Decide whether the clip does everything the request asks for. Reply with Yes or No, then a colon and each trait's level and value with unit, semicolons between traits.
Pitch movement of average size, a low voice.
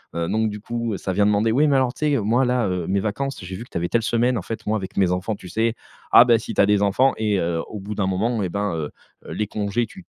Yes: average, 3.4 semitones; low, 105 Hz